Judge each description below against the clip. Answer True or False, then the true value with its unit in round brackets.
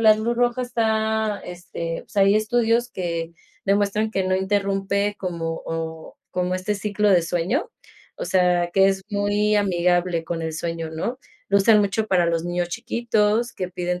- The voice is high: True (195 Hz)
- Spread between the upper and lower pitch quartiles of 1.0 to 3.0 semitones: False (3.5 semitones)